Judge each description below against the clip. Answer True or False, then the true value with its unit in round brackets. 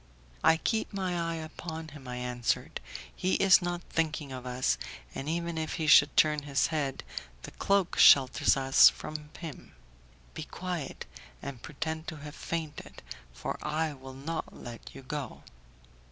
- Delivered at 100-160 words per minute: True (155 wpm)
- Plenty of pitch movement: False (3.5 semitones)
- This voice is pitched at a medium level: True (150 Hz)